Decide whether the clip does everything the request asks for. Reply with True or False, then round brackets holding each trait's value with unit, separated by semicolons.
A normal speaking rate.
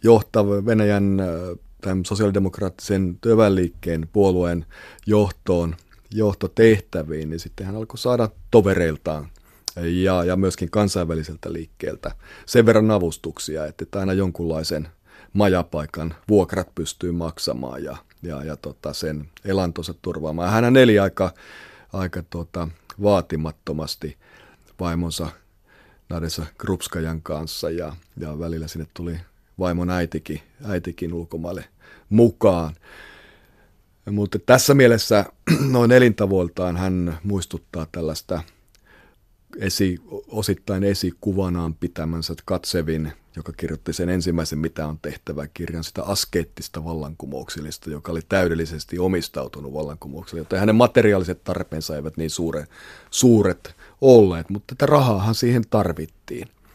True (105 wpm)